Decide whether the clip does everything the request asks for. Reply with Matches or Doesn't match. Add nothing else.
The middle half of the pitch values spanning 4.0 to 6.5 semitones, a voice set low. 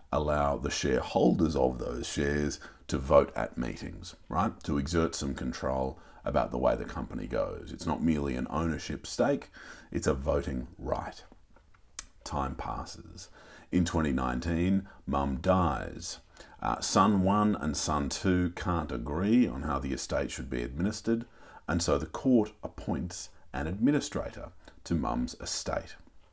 Matches